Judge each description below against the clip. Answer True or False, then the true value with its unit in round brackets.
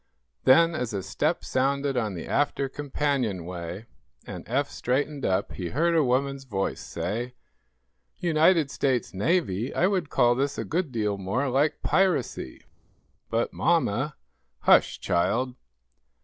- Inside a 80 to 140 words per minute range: True (135 wpm)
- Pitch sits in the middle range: False (130 Hz)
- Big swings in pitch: True (5.9 semitones)